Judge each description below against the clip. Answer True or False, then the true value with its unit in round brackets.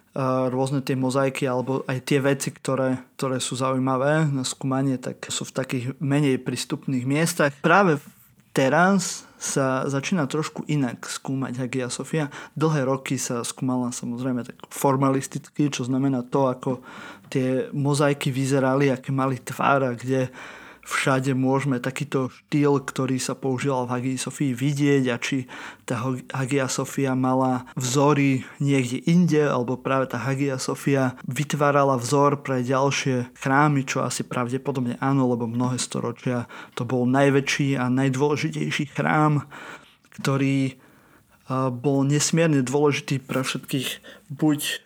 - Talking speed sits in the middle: True (130 wpm)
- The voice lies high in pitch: False (135 Hz)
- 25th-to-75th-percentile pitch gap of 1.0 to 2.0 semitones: True (1.7 semitones)